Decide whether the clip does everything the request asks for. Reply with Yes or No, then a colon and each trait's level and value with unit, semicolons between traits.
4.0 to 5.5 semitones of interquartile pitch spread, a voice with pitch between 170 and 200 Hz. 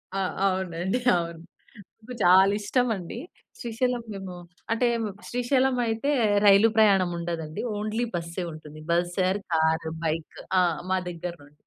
Yes: average, 4.9 semitones; high, 190 Hz